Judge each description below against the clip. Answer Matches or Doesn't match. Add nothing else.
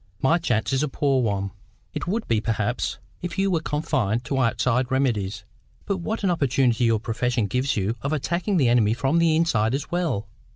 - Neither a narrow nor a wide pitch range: Doesn't match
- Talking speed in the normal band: Matches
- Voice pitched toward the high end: Doesn't match